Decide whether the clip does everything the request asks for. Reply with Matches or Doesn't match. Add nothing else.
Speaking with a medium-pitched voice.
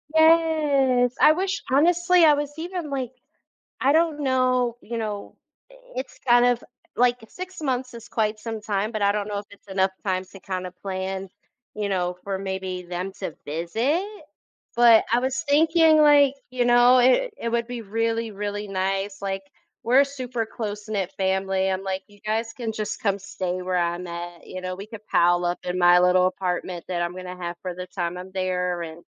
Doesn't match